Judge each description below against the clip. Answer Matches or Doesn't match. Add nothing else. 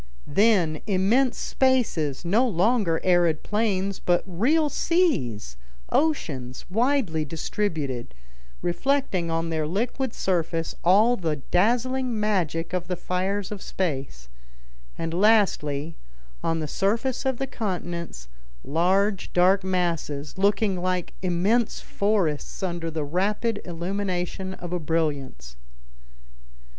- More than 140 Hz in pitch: Matches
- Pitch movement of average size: Matches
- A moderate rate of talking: Doesn't match